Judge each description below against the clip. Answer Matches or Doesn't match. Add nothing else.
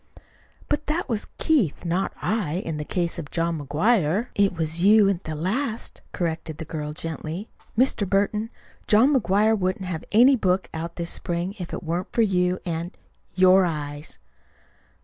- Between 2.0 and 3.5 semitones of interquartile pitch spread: Doesn't match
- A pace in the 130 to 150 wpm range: Doesn't match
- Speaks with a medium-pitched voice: Matches